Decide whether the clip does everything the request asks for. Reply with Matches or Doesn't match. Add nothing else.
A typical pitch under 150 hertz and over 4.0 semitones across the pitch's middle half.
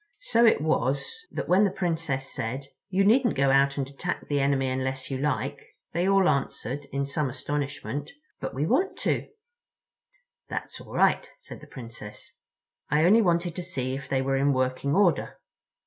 Matches